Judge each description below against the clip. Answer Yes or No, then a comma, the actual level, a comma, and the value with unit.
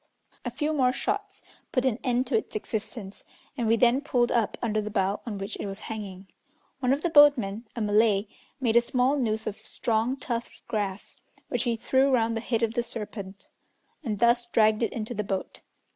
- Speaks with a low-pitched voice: No, high, 230 Hz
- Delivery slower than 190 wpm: No, average, 200 wpm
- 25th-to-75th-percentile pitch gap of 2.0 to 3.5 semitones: Yes, average, 2.9 semitones